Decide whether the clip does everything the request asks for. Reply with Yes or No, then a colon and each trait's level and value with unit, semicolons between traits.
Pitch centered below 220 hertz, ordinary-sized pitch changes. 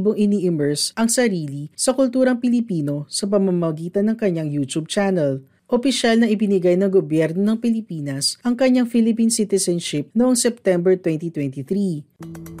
No: high, 190 Hz; wide, 6.1 semitones